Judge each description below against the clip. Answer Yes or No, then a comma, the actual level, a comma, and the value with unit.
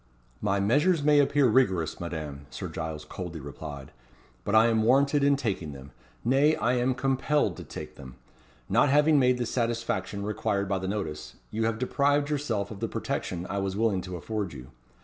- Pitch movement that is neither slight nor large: No, wide, 6.8 semitones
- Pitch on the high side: No, low, 110 Hz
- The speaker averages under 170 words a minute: No, average, 185 wpm